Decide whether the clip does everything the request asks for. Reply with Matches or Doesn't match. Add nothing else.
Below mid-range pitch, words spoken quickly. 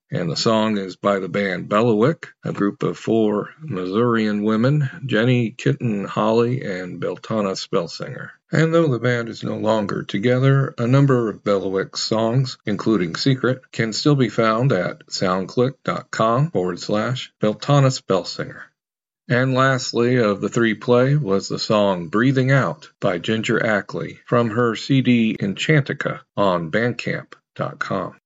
Doesn't match